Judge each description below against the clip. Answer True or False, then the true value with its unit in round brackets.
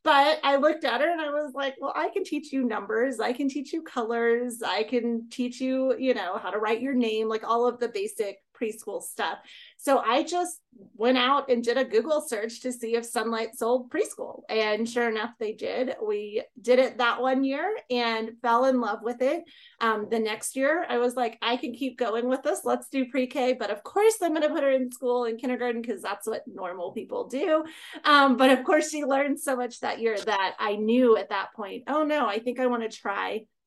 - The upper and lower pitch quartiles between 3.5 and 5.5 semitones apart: True (4.1 semitones)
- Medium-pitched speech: False (250 Hz)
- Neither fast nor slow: False (230 wpm)